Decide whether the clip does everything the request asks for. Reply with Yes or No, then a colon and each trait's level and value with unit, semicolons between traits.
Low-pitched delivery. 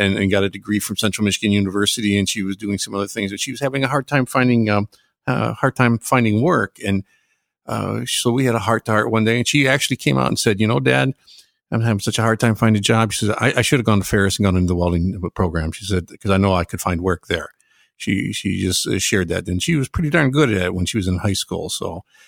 Yes: low, 105 Hz